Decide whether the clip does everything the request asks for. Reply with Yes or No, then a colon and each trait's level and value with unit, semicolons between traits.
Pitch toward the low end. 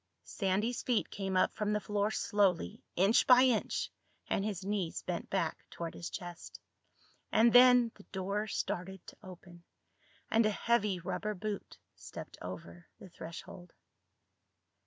No: high, 200 Hz